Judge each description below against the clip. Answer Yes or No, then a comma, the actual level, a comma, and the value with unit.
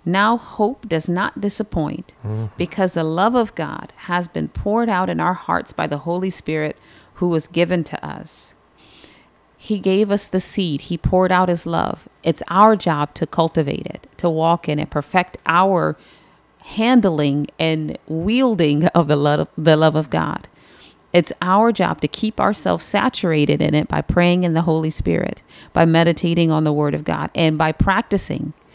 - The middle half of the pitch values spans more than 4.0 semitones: No, average, 3.3 semitones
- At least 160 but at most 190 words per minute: Yes, average, 170 wpm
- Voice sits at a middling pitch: Yes, medium, 170 Hz